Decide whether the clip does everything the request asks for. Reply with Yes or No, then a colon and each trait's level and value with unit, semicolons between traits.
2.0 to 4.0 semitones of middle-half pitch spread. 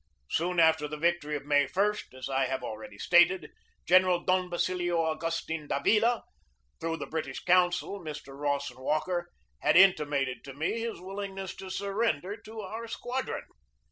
No: average, 4.4 semitones